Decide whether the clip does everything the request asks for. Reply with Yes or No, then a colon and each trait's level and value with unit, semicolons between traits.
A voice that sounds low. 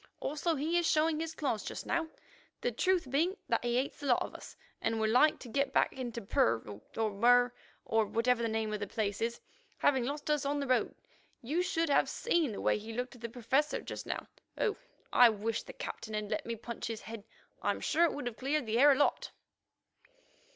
No: high, 245 Hz